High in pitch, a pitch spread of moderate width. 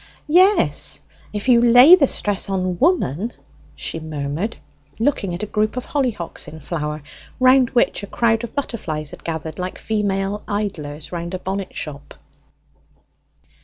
No: high, 200 Hz; wide, 6.4 semitones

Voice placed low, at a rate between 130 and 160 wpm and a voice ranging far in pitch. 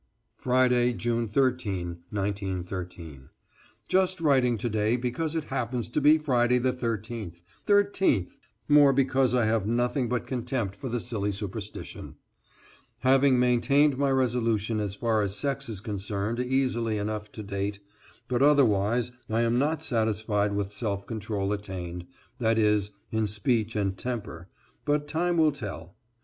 No: low, 115 Hz; average, 140 wpm; average, 3.9 semitones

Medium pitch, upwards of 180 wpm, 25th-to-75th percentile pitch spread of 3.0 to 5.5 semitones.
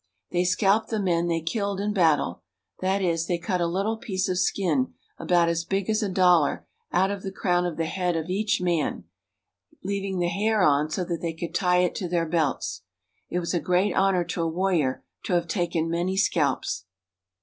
No: medium, 180 Hz; fast, 205 wpm; narrow, 2.4 semitones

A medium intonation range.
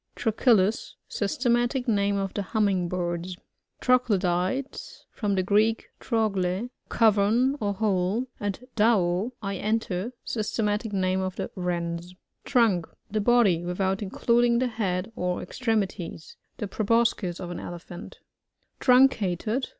Yes: average, 3.9 semitones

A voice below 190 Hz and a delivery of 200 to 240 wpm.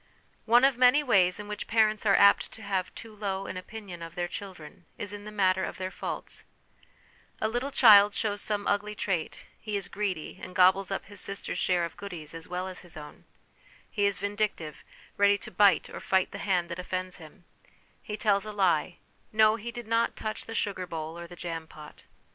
No: high, 200 Hz; fast, 205 wpm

